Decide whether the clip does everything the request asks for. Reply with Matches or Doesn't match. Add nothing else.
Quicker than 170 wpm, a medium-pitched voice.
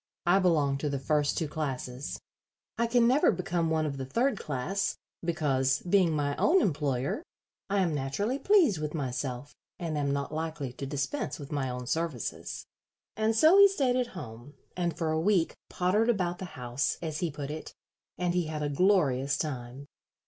Matches